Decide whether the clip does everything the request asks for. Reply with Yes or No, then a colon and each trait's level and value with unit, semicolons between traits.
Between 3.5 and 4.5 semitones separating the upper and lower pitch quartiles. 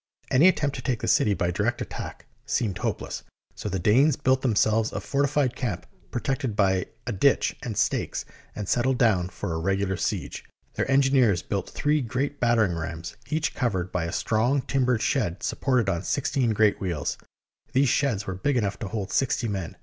No: wide, 5.5 semitones